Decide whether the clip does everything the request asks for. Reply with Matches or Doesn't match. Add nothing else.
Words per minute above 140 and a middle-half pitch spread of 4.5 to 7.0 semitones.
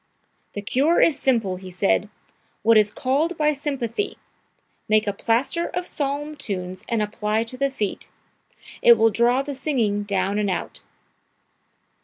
Matches